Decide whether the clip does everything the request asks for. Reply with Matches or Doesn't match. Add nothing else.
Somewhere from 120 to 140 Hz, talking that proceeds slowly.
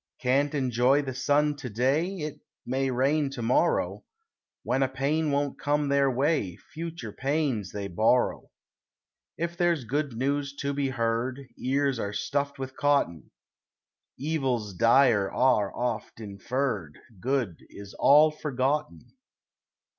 Matches